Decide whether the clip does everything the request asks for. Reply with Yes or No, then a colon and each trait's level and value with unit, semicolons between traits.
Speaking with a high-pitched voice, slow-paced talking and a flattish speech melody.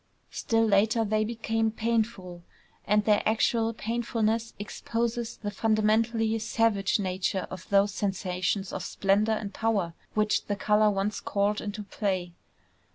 Yes: high, 215 Hz; slow, 130 wpm; narrow, 2.1 semitones